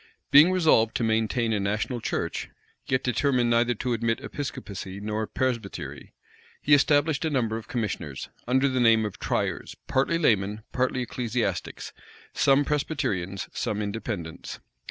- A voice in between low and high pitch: No, low, 115 Hz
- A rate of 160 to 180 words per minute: No, slow, 135 wpm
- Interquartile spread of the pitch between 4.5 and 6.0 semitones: No, average, 3.9 semitones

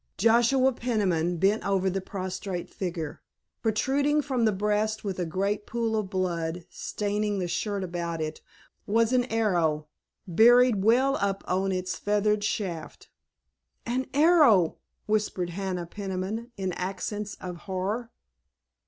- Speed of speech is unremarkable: No, slow, 130 wpm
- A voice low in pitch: No, high, 200 Hz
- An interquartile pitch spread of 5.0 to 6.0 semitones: No, average, 3.5 semitones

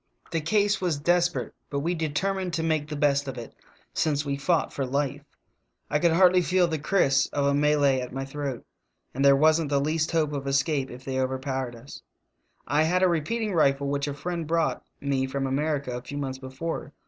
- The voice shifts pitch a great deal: No, average, 3.2 semitones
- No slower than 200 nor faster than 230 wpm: Yes, fast, 205 wpm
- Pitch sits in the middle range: Yes, medium, 145 Hz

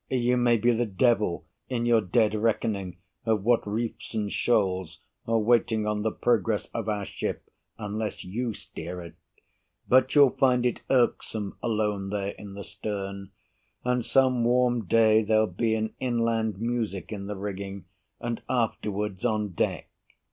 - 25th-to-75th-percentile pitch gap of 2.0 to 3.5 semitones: Yes, average, 2.9 semitones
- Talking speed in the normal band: Yes, average, 155 wpm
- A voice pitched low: Yes, low, 110 Hz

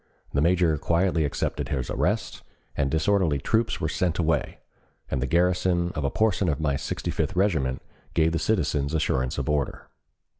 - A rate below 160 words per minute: No, average, 165 wpm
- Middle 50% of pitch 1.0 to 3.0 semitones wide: No, average, 4.2 semitones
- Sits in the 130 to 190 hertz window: No, very low, 80 Hz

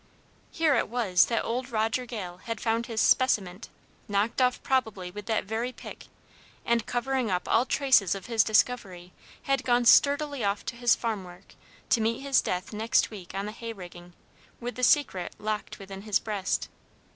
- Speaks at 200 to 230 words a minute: No, average, 180 wpm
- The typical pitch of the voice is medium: No, high, 225 Hz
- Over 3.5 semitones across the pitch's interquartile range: Yes, average, 3.9 semitones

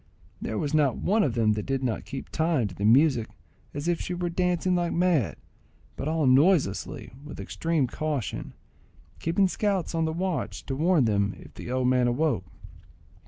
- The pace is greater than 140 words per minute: Yes, average, 185 wpm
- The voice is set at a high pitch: No, medium, 150 Hz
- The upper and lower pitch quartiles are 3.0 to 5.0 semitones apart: No, wide, 5.4 semitones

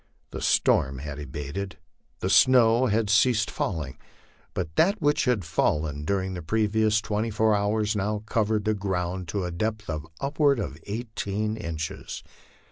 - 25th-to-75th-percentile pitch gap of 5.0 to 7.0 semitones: No, average, 4.5 semitones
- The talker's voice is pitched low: Yes, low, 105 Hz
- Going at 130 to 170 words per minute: Yes, average, 150 wpm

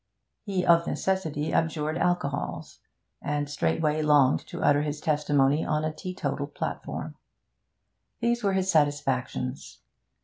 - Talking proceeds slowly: Yes, slow, 115 wpm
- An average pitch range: Yes, average, 3.3 semitones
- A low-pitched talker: No, medium, 150 Hz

